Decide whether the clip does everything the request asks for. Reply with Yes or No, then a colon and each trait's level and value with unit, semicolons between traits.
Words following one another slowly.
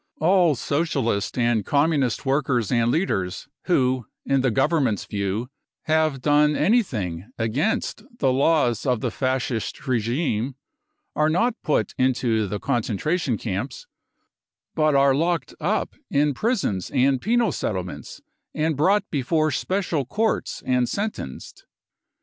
Yes: slow, 120 wpm